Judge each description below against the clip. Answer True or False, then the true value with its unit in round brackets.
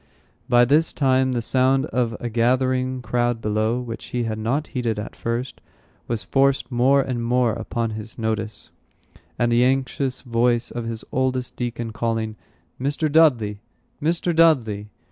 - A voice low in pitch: True (120 Hz)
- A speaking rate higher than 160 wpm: False (150 wpm)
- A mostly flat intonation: True (2.3 semitones)